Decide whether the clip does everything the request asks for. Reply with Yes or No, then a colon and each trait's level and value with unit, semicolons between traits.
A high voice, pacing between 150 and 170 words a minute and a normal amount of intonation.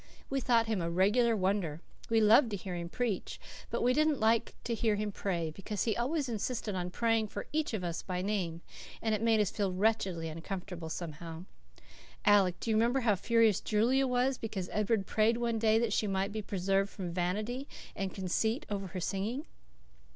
No: high, 210 Hz; average, 195 wpm; average, 3.7 semitones